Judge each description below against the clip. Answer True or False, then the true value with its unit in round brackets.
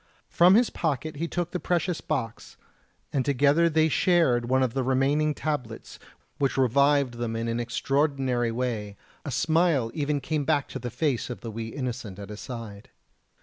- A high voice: False (135 Hz)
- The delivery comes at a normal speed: True (175 wpm)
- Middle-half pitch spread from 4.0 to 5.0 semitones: True (4.4 semitones)